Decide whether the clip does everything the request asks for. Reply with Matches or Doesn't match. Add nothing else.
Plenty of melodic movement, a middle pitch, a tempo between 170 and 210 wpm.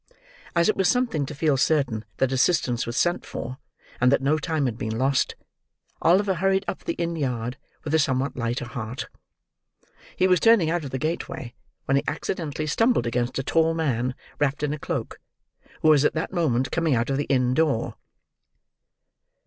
Doesn't match